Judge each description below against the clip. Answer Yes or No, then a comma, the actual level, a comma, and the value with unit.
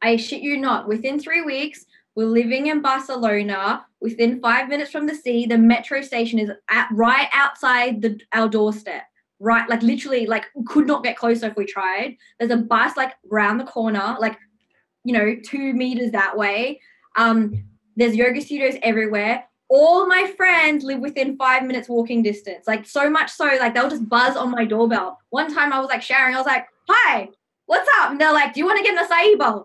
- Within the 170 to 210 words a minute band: Yes, average, 200 wpm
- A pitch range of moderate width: Yes, average, 3.7 semitones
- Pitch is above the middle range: Yes, high, 245 Hz